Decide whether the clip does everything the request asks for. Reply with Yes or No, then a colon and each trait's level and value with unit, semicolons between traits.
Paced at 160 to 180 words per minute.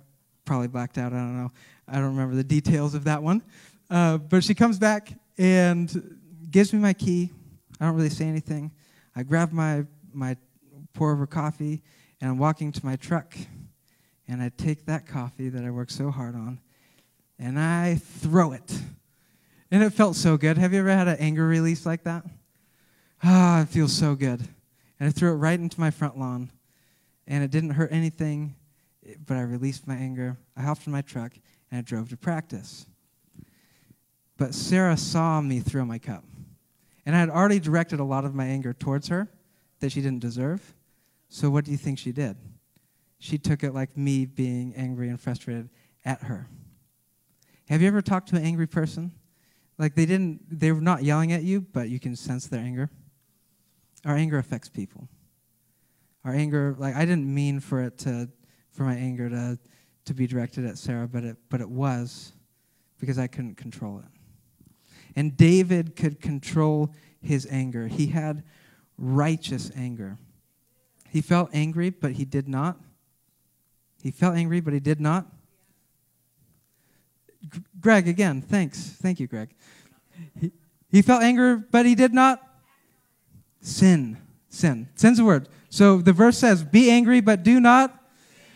Yes: average, 170 wpm